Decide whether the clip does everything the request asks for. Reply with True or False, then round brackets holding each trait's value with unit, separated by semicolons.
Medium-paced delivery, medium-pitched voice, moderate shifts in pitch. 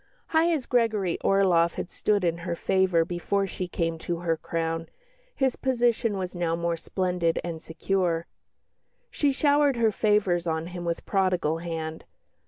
True (155 wpm; 180 Hz; 3.9 semitones)